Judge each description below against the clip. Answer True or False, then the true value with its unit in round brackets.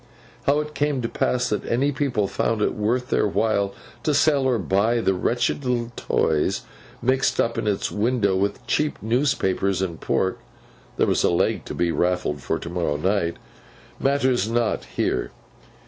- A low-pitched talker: True (115 Hz)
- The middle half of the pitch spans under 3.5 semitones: False (5.1 semitones)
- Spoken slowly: False (170 wpm)